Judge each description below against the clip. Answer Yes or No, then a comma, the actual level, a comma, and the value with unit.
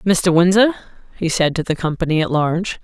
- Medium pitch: Yes, medium, 175 Hz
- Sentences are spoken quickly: No, average, 190 wpm